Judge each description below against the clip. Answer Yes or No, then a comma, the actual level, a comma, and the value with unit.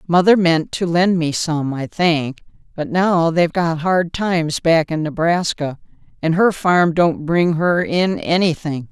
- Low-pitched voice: No, medium, 165 Hz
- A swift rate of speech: No, average, 170 wpm